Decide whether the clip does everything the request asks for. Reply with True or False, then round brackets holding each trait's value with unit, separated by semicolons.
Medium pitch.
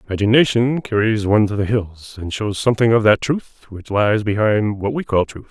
False (110 Hz)